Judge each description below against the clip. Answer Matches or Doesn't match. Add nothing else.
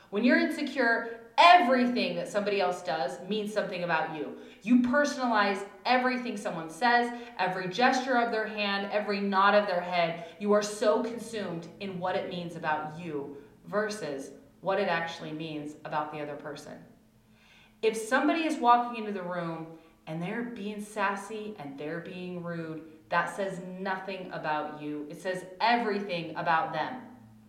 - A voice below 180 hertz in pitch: Doesn't match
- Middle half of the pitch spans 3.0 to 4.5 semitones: Doesn't match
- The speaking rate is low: Doesn't match